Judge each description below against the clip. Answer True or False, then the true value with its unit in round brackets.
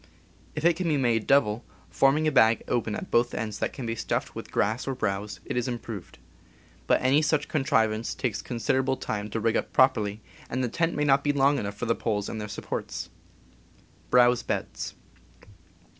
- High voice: False (120 Hz)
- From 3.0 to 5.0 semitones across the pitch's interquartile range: True (4.1 semitones)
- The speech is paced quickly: False (180 wpm)